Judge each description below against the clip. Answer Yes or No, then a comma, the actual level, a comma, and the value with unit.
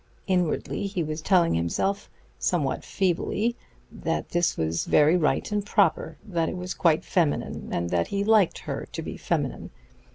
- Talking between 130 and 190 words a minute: Yes, average, 160 wpm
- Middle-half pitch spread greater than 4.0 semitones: Yes, average, 4.4 semitones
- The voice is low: No, medium, 175 Hz